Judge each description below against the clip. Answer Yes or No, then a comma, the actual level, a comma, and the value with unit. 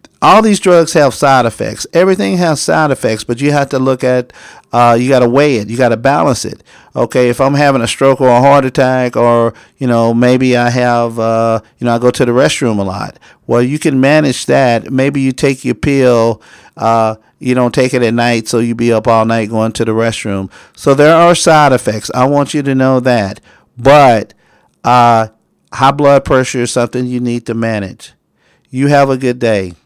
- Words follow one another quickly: Yes, fast, 215 wpm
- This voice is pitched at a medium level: No, low, 125 Hz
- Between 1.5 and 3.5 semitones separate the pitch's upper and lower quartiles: Yes, average, 2.9 semitones